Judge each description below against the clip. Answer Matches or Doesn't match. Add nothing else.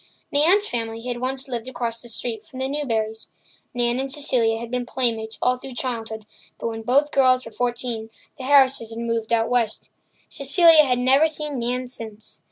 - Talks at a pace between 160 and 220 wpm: Matches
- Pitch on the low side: Doesn't match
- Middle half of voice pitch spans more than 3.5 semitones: Doesn't match